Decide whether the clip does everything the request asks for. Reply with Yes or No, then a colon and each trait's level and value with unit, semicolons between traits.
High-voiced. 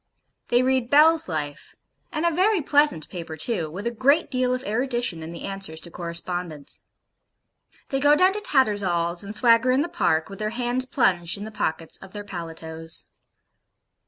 Yes: high, 215 Hz